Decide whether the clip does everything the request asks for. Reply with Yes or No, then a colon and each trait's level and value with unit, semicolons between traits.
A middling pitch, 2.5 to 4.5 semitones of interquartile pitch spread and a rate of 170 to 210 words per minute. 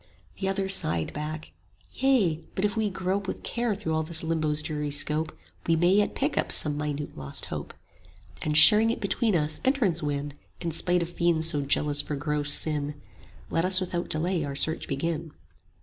Yes: medium, 160 Hz; average, 4.1 semitones; average, 190 wpm